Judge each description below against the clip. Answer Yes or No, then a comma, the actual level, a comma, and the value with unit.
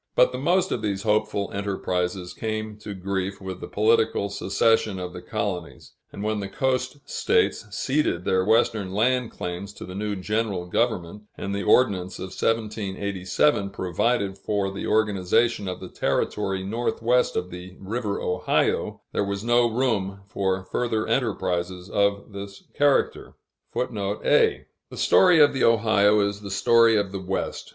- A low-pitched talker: Yes, low, 100 Hz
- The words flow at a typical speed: Yes, average, 150 wpm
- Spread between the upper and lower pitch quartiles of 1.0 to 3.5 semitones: Yes, average, 3.1 semitones